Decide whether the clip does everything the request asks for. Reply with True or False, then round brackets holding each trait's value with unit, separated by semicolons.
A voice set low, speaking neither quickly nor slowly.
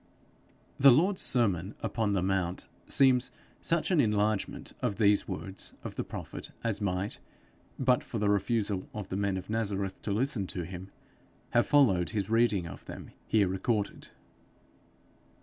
True (105 Hz; 150 wpm)